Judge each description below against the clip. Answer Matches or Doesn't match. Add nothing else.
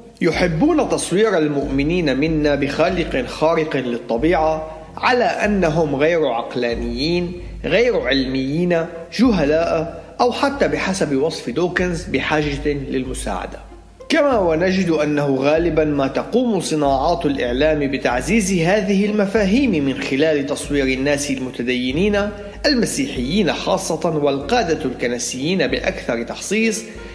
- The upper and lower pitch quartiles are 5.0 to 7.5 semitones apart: Matches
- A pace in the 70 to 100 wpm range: Matches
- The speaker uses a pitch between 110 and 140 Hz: Doesn't match